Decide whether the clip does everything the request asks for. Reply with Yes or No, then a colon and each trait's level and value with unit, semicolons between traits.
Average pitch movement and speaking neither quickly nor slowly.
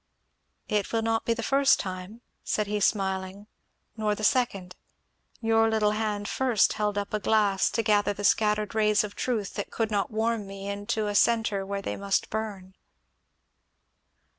No: narrow, 1.7 semitones; average, 165 wpm